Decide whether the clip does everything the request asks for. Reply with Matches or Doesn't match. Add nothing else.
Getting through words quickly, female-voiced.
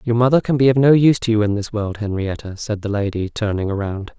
Doesn't match